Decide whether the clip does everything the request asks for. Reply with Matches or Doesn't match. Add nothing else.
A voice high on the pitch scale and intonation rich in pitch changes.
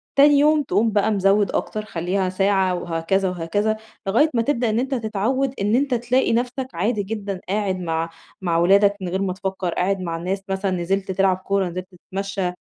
Doesn't match